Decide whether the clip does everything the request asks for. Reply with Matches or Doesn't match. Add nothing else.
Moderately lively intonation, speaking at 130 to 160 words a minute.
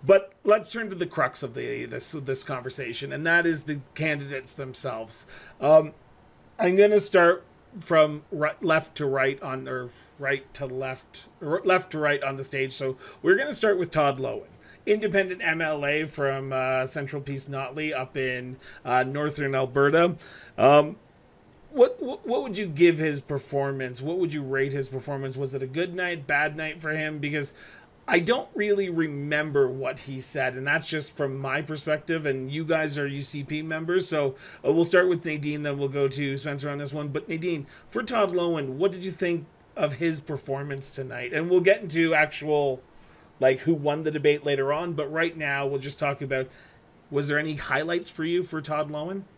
Doesn't match